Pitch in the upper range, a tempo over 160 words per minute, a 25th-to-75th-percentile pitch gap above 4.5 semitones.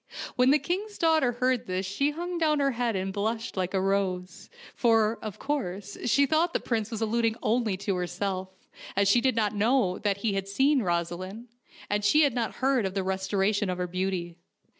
Yes: high, 215 Hz; fast, 205 wpm; average, 5.1 semitones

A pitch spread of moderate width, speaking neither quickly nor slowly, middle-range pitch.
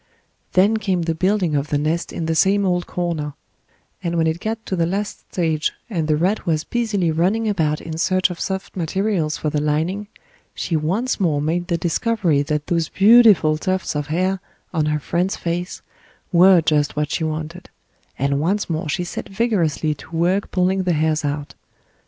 Yes: average, 3.6 semitones; average, 185 wpm; medium, 170 Hz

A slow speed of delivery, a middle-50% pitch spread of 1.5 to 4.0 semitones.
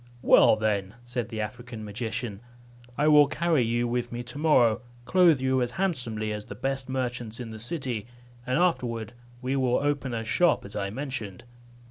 No: average, 175 wpm; average, 3.4 semitones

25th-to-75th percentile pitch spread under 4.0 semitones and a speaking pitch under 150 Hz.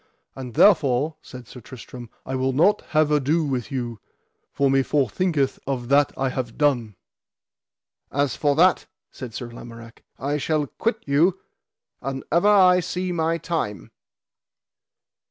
No: average, 4.3 semitones; medium, 140 Hz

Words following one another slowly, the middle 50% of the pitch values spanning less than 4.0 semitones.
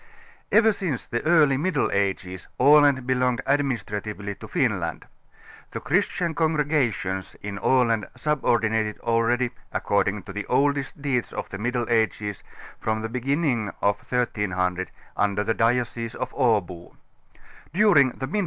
No: slow, 120 wpm; average, 5.0 semitones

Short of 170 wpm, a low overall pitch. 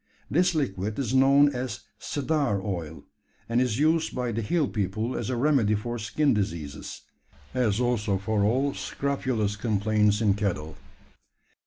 Yes: average, 145 wpm; low, 115 Hz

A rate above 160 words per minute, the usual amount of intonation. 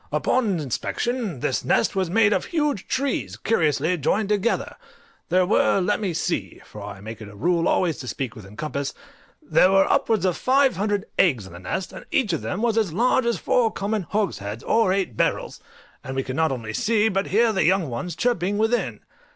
No: average, 200 wpm; wide, 8.4 semitones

